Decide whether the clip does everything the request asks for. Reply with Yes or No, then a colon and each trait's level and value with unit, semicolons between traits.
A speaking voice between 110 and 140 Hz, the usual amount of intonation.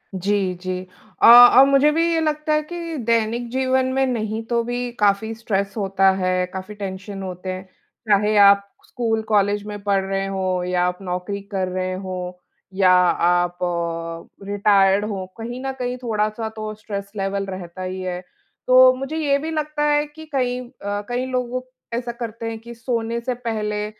No: high, 215 Hz; average, 4.3 semitones